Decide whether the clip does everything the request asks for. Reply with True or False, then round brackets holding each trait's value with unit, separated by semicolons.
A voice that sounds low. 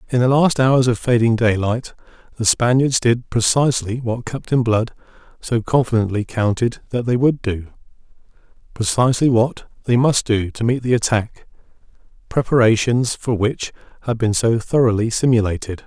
True (120 Hz)